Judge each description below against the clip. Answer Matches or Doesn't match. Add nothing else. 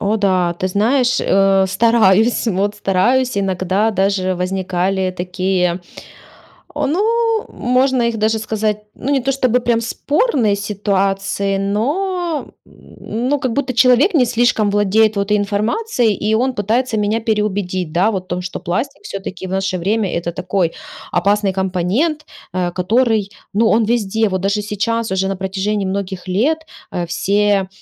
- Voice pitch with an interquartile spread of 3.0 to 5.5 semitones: Matches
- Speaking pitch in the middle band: Doesn't match